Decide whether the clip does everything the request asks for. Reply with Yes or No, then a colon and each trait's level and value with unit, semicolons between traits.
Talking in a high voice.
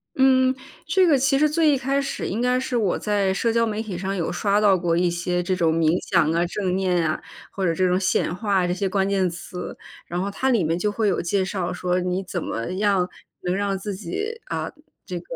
Yes: high, 195 Hz